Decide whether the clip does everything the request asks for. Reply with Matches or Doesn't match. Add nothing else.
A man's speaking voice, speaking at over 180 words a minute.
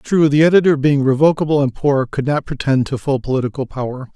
Matches